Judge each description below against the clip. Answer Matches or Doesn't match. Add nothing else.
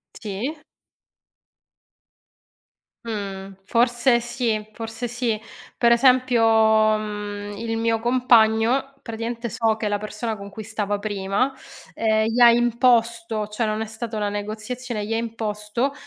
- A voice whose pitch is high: Matches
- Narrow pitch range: Matches